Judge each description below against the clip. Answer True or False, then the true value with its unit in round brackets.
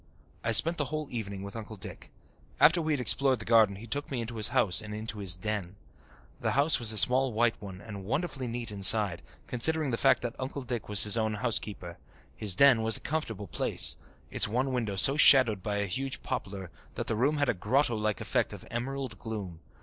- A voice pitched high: False (115 Hz)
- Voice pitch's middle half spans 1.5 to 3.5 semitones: False (4.2 semitones)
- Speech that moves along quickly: True (215 wpm)